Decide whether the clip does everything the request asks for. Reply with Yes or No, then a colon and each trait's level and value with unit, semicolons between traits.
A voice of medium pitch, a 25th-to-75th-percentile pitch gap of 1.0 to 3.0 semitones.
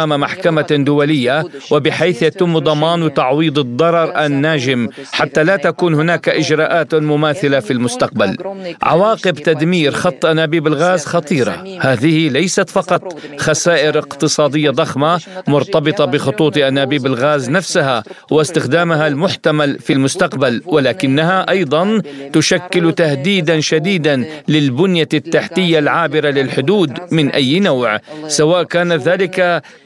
Yes: medium, 155 Hz; average, 2.7 semitones